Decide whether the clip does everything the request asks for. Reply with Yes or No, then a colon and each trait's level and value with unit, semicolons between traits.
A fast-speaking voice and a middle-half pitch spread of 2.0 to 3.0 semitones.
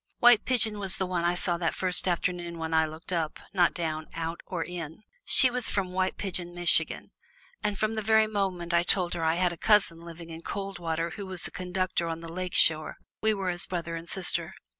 Yes: fast, 220 wpm; narrow, 2.6 semitones